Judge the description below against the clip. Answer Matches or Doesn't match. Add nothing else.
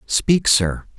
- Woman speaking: Doesn't match